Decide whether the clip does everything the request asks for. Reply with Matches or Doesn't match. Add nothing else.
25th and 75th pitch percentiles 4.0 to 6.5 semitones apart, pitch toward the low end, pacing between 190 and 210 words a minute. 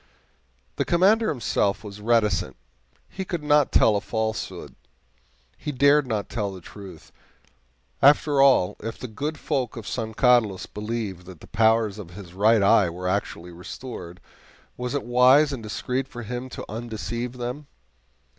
Doesn't match